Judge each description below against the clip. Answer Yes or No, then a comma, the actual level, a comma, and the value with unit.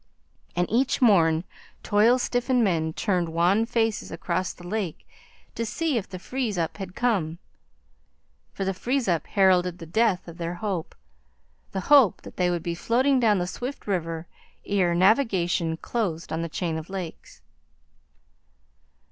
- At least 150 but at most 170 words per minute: Yes, average, 155 wpm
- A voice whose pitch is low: No, high, 190 Hz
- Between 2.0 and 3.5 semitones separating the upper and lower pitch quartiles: No, average, 4.9 semitones